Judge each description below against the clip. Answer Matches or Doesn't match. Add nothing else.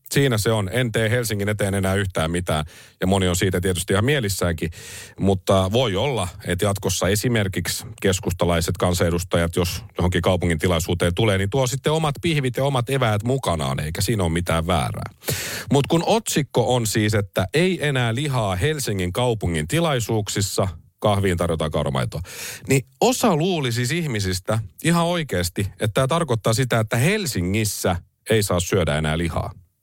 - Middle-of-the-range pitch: Doesn't match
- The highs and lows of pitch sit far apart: Matches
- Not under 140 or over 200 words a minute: Matches